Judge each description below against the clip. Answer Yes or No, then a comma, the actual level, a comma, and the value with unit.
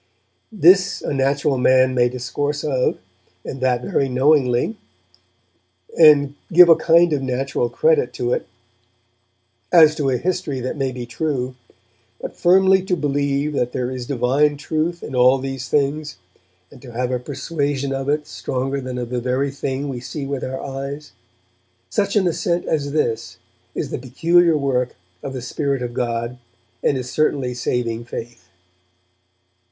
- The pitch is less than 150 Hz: Yes, low, 135 Hz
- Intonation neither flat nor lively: Yes, average, 3.2 semitones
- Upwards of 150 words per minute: Yes, average, 160 wpm